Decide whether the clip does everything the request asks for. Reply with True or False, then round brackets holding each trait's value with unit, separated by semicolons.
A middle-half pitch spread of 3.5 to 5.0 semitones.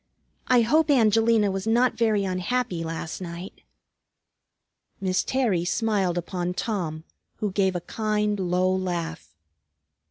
True (4.1 semitones)